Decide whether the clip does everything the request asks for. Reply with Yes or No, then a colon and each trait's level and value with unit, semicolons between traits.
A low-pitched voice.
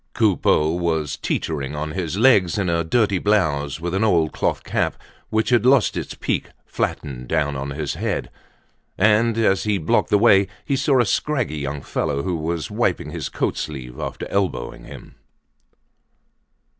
Yes: very low, 85 Hz